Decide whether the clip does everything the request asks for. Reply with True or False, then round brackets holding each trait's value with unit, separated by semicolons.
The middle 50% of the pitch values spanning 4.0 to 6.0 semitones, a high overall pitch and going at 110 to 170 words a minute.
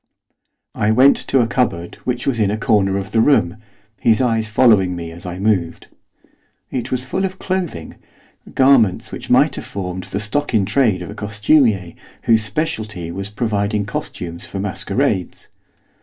False (4.7 semitones; 105 Hz; 165 wpm)